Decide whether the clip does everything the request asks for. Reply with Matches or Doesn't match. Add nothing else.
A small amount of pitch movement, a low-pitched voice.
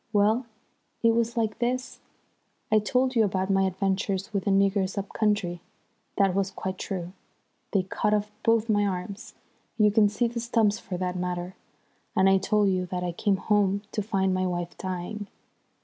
Doesn't match